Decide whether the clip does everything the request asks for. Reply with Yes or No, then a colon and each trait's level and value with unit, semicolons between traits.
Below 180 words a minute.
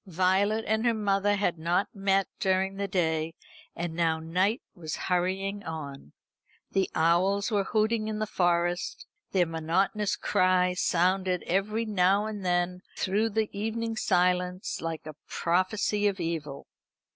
Yes: average, 140 wpm